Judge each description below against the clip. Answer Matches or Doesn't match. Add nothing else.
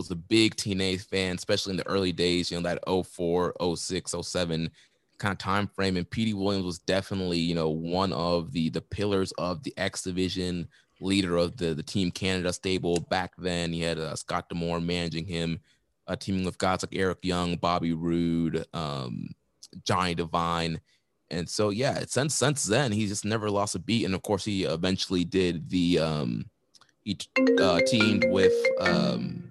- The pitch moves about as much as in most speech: Doesn't match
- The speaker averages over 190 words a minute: Doesn't match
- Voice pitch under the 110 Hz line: Matches